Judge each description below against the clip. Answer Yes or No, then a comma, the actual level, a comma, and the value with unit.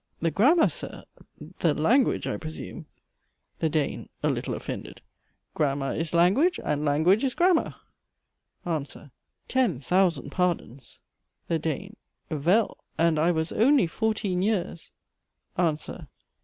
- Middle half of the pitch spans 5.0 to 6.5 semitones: Yes, wide, 5.6 semitones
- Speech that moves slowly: Yes, slow, 120 wpm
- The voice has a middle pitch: Yes, medium, 170 Hz